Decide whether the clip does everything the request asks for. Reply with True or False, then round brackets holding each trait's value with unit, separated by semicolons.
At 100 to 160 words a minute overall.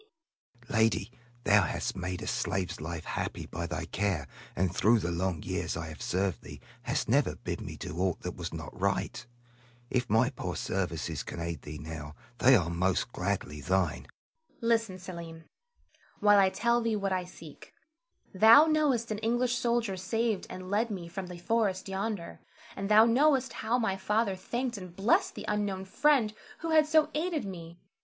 False (180 wpm)